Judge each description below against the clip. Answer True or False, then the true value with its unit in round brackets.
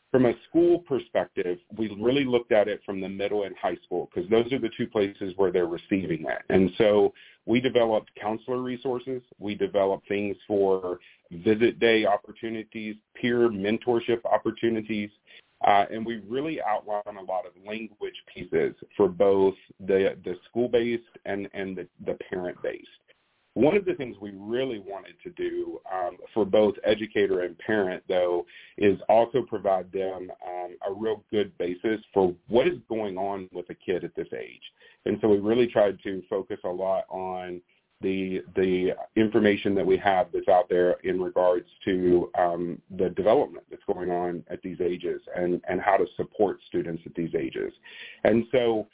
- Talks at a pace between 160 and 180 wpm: True (170 wpm)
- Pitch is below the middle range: True (110 Hz)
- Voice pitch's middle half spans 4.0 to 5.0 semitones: True (4.7 semitones)